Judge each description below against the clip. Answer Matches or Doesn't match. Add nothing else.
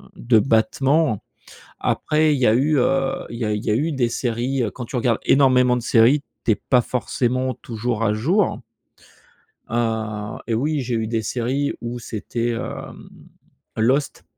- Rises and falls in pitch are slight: Doesn't match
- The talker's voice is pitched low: Matches